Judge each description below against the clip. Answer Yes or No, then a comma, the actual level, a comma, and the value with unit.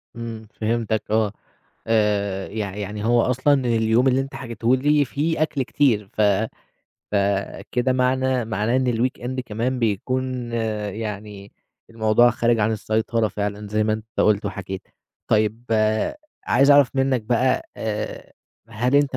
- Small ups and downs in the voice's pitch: No, average, 3.3 semitones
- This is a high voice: No, low, 115 Hz